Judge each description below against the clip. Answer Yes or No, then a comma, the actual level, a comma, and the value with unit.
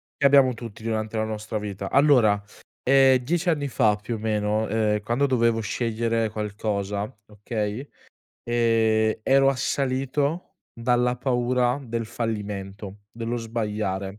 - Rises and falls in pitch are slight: No, average, 3.1 semitones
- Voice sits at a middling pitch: No, low, 115 Hz